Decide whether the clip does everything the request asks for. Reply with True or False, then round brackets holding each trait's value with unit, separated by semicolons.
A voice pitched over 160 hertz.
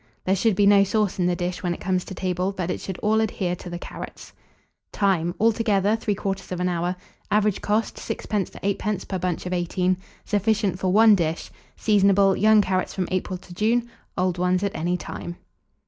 True (190 Hz)